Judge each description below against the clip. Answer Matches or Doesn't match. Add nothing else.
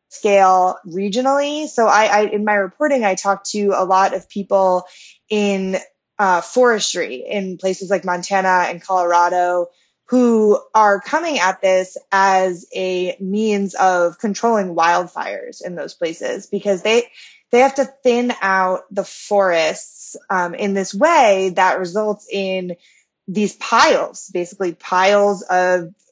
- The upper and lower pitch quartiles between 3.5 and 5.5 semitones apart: Doesn't match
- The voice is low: Doesn't match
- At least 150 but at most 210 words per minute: Doesn't match